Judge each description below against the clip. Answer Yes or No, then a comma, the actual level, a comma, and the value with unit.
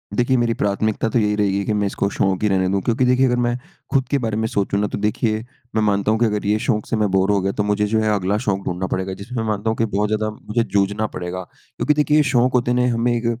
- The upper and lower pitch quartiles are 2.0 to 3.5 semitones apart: Yes, average, 2.9 semitones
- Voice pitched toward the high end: No, low, 105 Hz